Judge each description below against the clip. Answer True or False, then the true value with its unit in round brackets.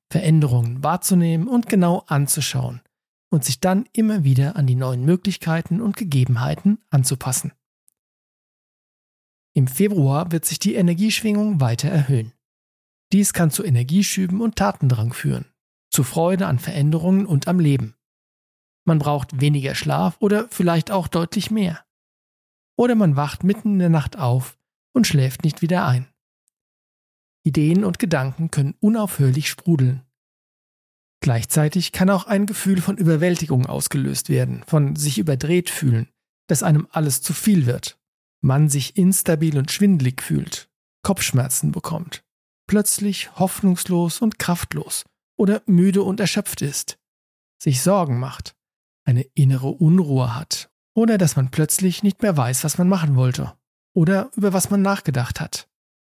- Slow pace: False (135 wpm)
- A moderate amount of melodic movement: False (6.0 semitones)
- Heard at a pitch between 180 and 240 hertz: False (160 Hz)